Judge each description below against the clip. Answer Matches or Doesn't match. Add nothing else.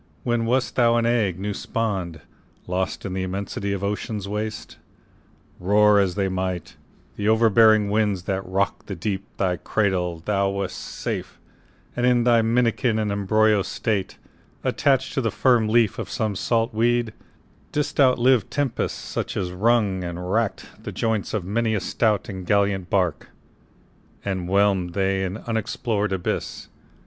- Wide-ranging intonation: Doesn't match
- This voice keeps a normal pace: Matches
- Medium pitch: Doesn't match